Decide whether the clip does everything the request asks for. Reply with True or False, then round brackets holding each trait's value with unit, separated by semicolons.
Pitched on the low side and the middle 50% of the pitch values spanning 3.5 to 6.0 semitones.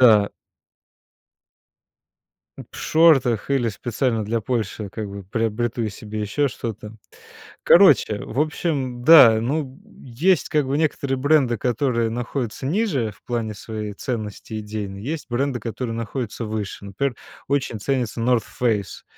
True (120 Hz; 4.1 semitones)